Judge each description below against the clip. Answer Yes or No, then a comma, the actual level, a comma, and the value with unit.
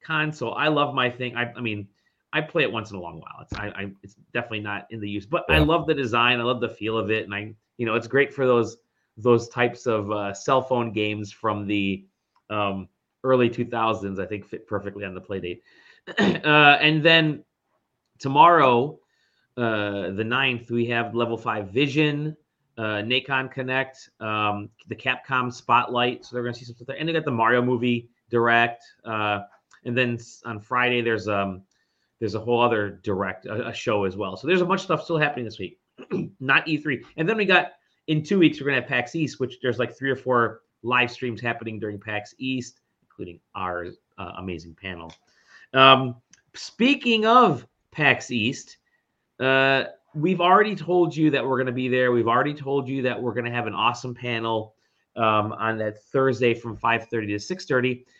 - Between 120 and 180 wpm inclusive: No, average, 200 wpm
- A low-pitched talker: Yes, low, 120 Hz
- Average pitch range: Yes, average, 3.6 semitones